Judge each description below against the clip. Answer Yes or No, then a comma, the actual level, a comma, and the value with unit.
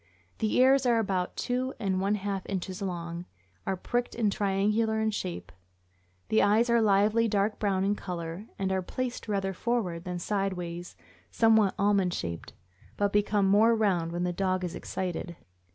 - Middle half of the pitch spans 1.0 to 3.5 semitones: Yes, average, 3.2 semitones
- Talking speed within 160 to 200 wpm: Yes, average, 170 wpm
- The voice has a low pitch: No, high, 195 Hz